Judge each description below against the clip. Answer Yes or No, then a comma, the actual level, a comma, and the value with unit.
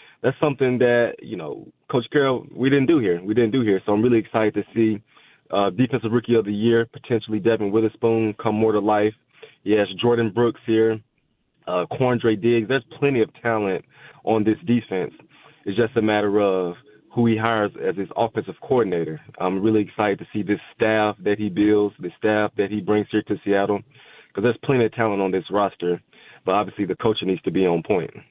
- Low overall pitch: Yes, low, 110 Hz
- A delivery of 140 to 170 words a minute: No, average, 200 wpm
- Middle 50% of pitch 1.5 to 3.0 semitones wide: Yes, narrow, 2.4 semitones